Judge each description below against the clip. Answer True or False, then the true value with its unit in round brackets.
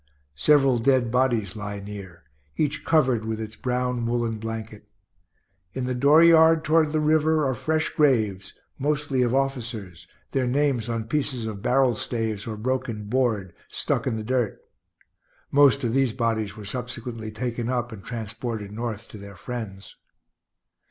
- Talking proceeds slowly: False (150 wpm)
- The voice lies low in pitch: True (120 Hz)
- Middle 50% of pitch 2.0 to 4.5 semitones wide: True (3.5 semitones)